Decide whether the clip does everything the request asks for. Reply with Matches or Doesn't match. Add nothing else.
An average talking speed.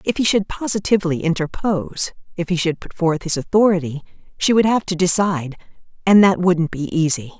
Matches